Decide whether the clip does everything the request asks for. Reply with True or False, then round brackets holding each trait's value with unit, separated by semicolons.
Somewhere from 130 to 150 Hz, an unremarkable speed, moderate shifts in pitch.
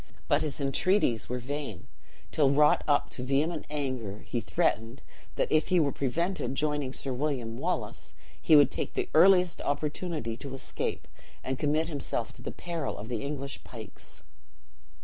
True (140 Hz; 160 wpm; 3.6 semitones)